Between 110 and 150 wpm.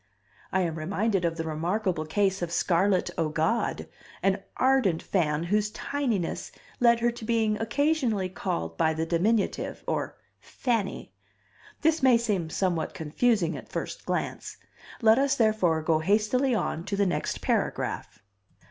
Yes: average, 140 wpm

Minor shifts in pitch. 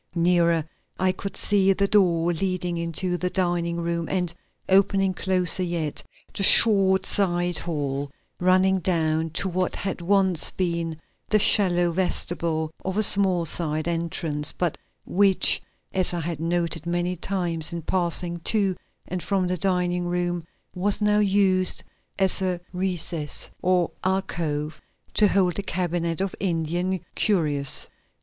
Yes: narrow, 2.1 semitones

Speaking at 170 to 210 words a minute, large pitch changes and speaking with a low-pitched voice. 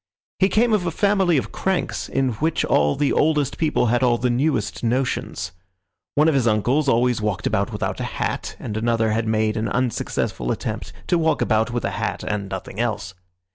Yes: average, 195 wpm; wide, 5.7 semitones; low, 120 Hz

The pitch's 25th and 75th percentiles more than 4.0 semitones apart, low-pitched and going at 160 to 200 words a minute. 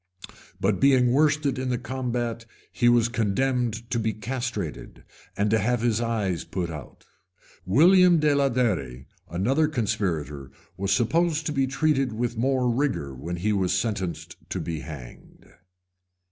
No: wide, 5.5 semitones; low, 120 Hz; average, 145 wpm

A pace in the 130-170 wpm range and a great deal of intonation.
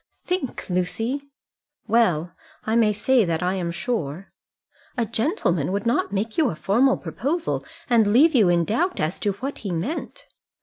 Yes: average, 165 wpm; wide, 6.2 semitones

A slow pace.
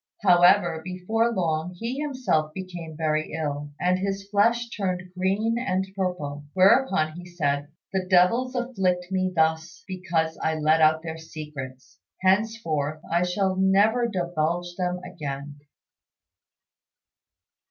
Yes: slow, 120 wpm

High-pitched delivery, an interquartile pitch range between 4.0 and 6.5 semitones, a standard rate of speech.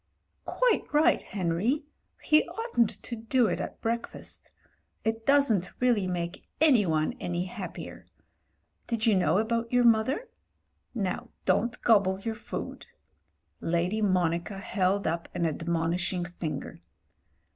No: high, 205 Hz; average, 5.1 semitones; slow, 125 wpm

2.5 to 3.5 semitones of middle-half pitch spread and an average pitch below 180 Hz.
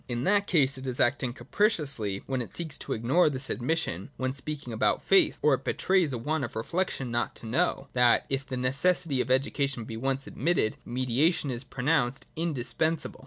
No: average, 4.4 semitones; low, 135 Hz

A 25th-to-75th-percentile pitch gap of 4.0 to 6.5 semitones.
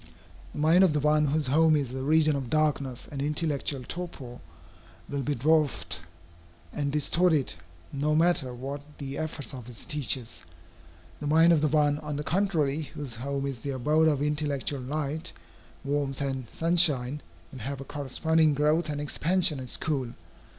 No: narrow, 2.4 semitones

